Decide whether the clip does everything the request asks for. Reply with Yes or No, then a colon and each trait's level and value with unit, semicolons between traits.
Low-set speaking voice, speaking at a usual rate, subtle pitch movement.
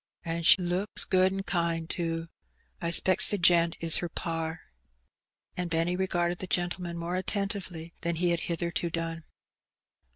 No: medium, 170 Hz; average, 155 wpm; narrow, 1.3 semitones